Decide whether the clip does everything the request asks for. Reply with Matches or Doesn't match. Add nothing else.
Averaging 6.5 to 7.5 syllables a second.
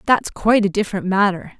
Doesn't match